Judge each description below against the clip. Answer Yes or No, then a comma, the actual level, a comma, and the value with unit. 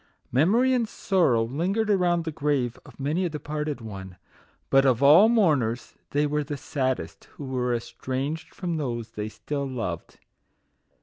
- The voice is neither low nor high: Yes, medium, 145 Hz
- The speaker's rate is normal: Yes, average, 165 wpm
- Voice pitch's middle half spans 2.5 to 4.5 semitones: No, average, 5.1 semitones